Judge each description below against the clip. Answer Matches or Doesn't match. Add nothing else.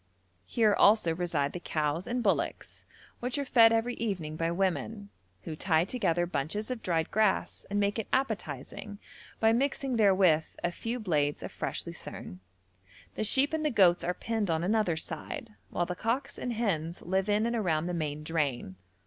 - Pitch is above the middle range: Matches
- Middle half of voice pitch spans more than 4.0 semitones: Matches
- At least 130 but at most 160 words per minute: Doesn't match